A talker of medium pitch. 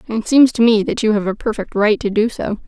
No: high, 220 Hz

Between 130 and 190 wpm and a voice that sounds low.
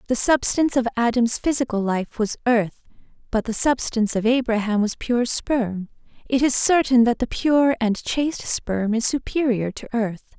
No: average, 170 wpm; high, 235 Hz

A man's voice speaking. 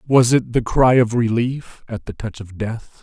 Yes: male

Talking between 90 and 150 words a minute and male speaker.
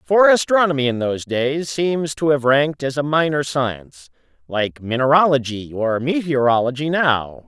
Yes: average, 145 wpm; male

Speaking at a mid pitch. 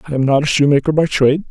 Yes: medium, 145 Hz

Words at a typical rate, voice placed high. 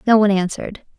Yes: average, 180 wpm; high, 205 Hz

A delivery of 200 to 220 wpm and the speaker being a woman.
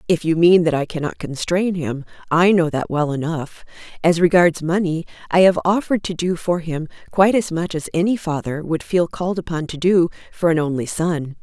Yes: fast, 205 wpm; female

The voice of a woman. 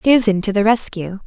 Yes: female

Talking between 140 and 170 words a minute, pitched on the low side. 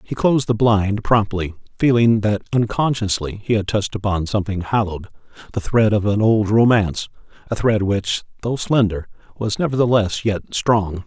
Yes: average, 155 wpm; low, 105 Hz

